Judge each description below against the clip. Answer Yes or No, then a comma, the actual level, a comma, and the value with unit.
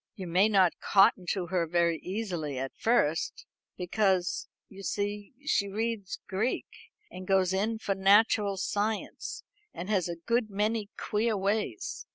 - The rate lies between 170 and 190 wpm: No, average, 145 wpm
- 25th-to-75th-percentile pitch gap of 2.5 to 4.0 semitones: Yes, average, 2.8 semitones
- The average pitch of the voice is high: Yes, high, 195 Hz